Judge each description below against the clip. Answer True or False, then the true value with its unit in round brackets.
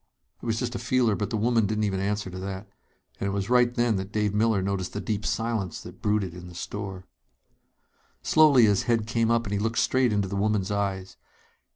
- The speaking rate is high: True (220 wpm)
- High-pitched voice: False (105 Hz)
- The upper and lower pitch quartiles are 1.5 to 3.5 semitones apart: True (2.8 semitones)